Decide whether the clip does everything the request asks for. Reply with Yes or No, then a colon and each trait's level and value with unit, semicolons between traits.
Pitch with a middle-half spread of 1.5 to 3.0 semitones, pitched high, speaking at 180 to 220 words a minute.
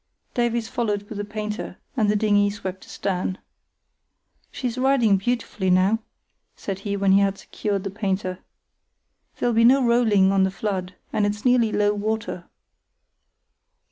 No: narrow, 2.4 semitones; high, 205 Hz; average, 145 wpm